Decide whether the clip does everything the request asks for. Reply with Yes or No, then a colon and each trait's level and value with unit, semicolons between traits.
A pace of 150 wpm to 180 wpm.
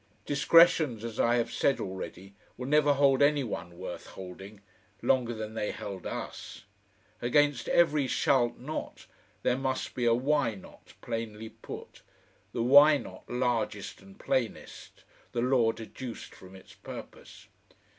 No: average, 140 wpm